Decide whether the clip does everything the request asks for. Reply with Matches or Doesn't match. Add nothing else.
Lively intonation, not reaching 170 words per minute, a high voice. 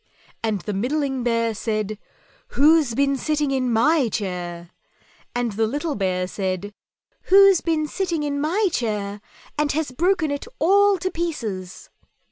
Matches